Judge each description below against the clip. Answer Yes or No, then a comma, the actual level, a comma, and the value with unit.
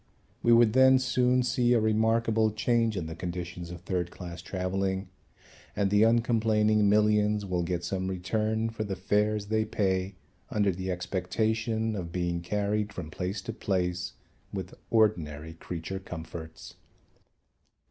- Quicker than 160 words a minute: No, average, 140 wpm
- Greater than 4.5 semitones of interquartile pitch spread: No, average, 3.5 semitones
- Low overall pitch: Yes, low, 100 Hz